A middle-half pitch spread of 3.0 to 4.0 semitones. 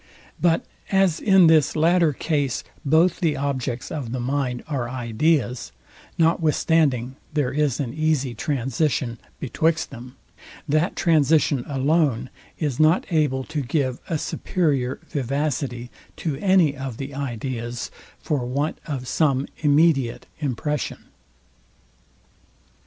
Yes: average, 3.6 semitones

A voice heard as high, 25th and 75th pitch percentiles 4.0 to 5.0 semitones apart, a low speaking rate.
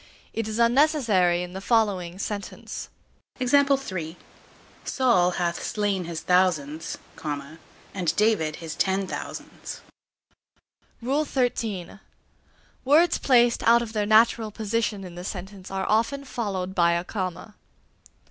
Yes: high, 200 Hz; average, 4.4 semitones; slow, 110 wpm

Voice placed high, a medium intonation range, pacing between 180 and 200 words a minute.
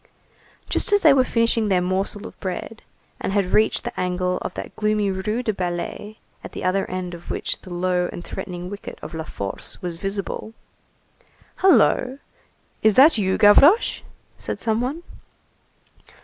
No: high, 200 Hz; average, 3.8 semitones; average, 165 wpm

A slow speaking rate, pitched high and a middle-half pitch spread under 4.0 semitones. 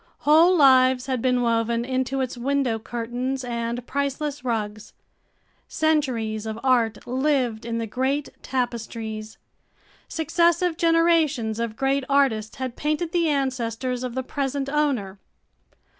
Yes: slow, 125 wpm; very high, 255 Hz; average, 3.4 semitones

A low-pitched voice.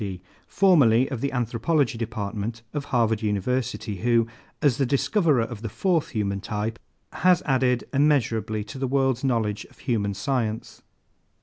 Yes: low, 120 Hz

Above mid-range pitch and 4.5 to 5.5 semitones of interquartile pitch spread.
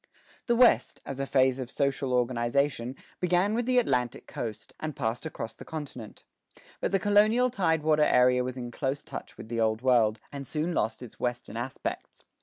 No: low, 130 Hz; average, 4.9 semitones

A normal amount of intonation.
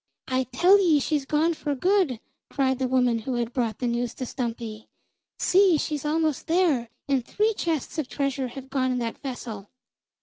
Yes: average, 4.2 semitones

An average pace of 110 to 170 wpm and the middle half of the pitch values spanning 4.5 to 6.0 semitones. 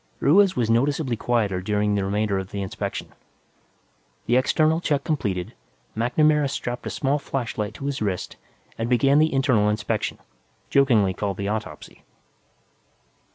Yes: average, 140 wpm; average, 5.1 semitones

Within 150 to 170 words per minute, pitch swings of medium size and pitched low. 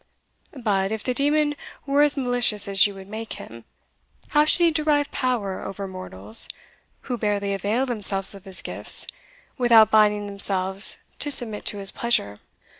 No: average, 160 wpm; average, 4.6 semitones; high, 210 Hz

